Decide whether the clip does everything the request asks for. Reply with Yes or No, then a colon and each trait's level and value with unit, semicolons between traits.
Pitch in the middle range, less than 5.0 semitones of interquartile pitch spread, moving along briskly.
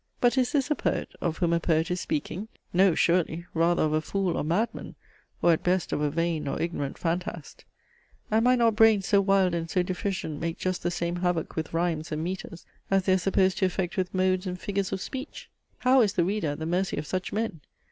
Yes: medium, 180 Hz; average, 2.9 semitones; fast, 230 wpm